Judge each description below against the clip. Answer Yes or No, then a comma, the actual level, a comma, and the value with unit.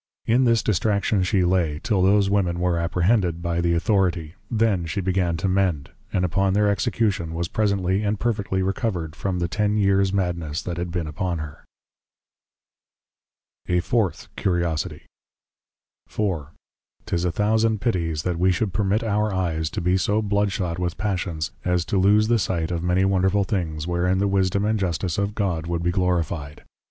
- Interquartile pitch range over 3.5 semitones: No, average, 2.9 semitones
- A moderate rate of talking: Yes, average, 170 wpm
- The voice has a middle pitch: No, very low, 95 Hz